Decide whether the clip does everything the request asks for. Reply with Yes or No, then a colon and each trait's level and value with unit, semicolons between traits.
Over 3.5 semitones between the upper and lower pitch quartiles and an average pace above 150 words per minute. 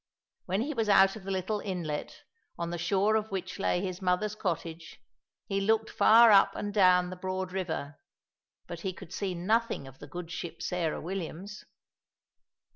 No: average, 2.9 semitones; average, 175 wpm